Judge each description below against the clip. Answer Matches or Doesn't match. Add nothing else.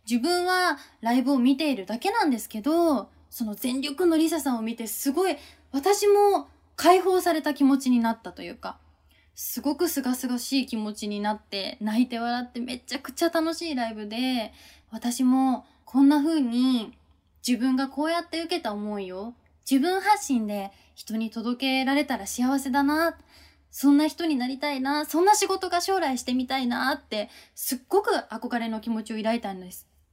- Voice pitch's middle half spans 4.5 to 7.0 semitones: Matches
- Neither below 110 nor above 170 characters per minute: Doesn't match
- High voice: Matches